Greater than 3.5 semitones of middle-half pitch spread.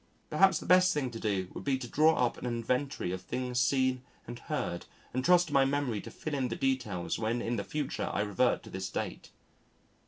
Yes: average, 4.0 semitones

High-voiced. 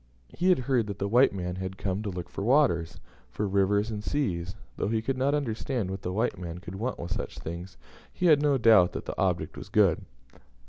No: low, 100 Hz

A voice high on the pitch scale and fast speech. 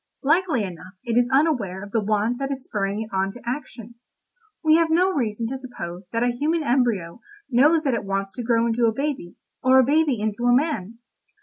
Yes: high, 240 Hz; fast, 210 wpm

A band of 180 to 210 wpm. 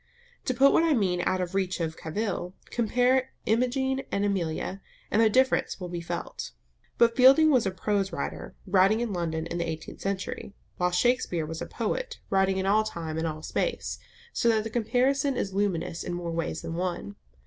Yes: average, 190 wpm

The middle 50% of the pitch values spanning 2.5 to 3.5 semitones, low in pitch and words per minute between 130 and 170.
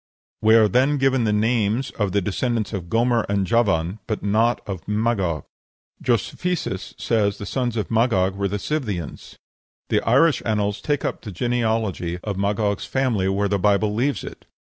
Yes: average, 3.1 semitones; low, 105 Hz; average, 165 wpm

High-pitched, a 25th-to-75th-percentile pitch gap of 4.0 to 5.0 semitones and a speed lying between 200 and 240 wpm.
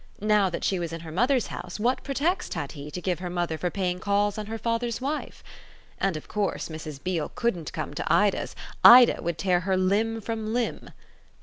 Yes: high, 195 Hz; average, 4.6 semitones; fast, 205 wpm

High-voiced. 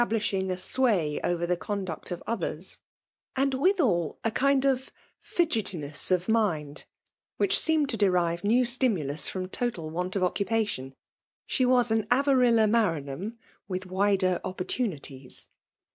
Yes: high, 200 Hz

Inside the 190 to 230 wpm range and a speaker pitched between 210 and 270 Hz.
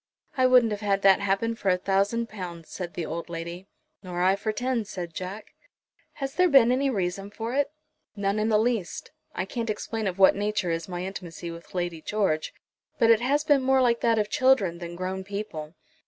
No: fast, 205 wpm; high, 200 Hz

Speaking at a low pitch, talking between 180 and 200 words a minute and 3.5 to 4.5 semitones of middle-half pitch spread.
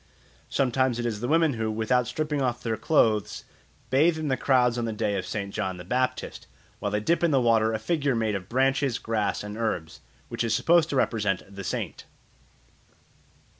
Yes: low, 120 Hz; average, 190 wpm; average, 3.9 semitones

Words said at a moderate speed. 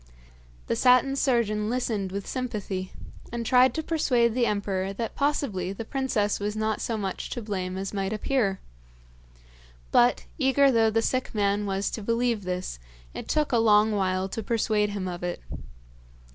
Yes: average, 165 wpm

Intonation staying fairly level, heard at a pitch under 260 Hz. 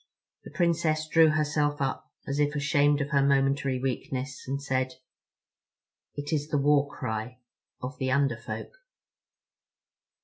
Yes: narrow, 1.8 semitones; medium, 140 Hz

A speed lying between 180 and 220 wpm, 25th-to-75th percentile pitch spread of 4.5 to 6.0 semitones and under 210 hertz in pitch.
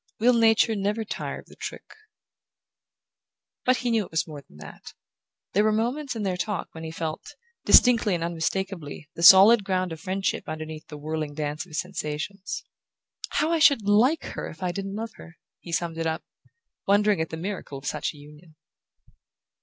Yes: average, 185 wpm; average, 5.0 semitones; medium, 185 Hz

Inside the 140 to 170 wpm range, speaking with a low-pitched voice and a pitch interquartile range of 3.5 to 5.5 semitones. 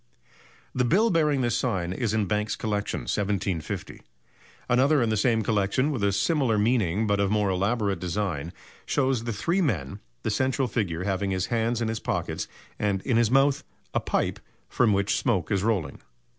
No: average, 180 wpm; low, 105 Hz; average, 3.8 semitones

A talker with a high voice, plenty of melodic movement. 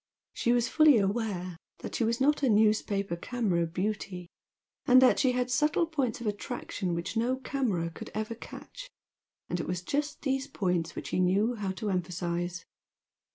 Yes: high, 215 Hz; wide, 5.9 semitones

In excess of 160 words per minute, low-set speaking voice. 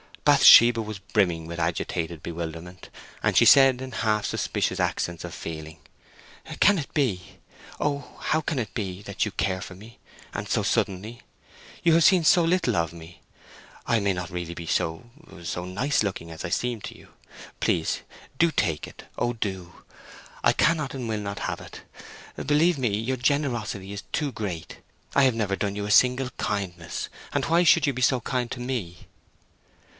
Yes: average, 175 wpm; low, 105 Hz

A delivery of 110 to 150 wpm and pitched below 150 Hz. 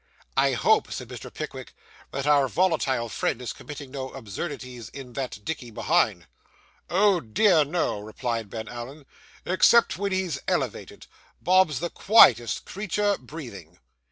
Yes: slow, 135 wpm; medium, 140 Hz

